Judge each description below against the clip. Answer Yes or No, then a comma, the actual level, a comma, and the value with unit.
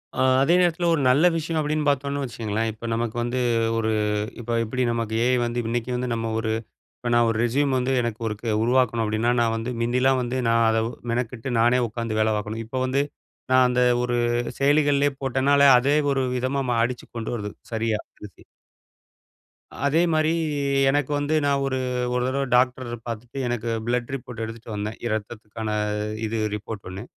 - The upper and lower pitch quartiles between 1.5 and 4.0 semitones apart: Yes, average, 2.9 semitones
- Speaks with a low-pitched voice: Yes, low, 120 Hz